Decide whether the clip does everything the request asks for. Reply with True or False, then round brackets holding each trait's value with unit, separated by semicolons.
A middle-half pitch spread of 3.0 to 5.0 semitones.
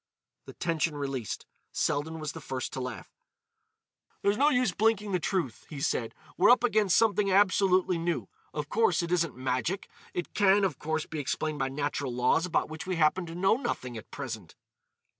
False (5.6 semitones)